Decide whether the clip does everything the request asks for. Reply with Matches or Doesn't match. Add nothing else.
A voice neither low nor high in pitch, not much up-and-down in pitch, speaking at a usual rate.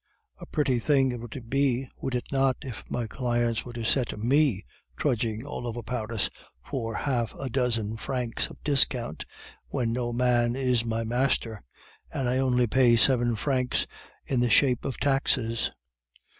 Doesn't match